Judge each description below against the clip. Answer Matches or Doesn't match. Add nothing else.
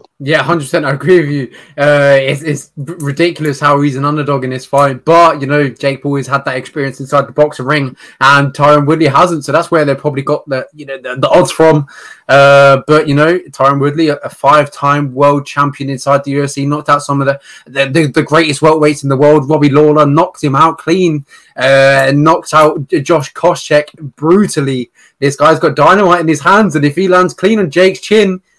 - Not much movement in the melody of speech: Matches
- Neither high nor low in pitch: Matches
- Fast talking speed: Matches